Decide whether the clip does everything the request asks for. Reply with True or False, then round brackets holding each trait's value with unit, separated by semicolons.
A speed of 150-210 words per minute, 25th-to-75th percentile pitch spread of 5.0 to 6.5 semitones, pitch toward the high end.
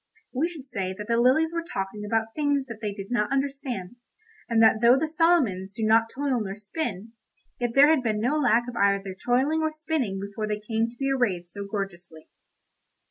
True (200 wpm; 5.3 semitones; 230 Hz)